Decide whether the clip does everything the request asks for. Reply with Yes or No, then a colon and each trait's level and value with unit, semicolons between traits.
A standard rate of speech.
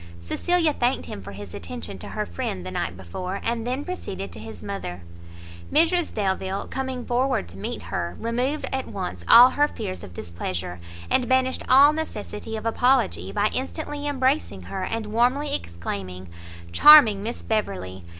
Yes: average, 160 wpm